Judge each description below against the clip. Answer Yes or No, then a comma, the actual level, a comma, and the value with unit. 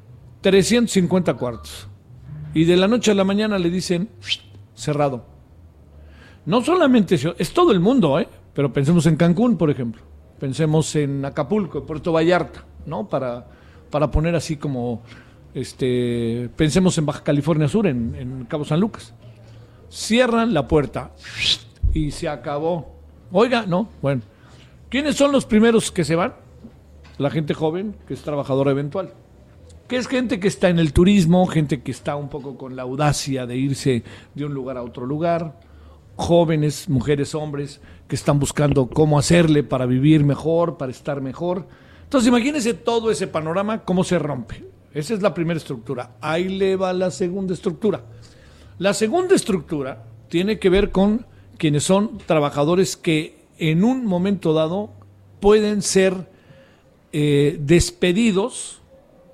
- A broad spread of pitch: Yes, wide, 6.4 semitones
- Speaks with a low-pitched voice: No, medium, 155 Hz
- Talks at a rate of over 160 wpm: No, average, 150 wpm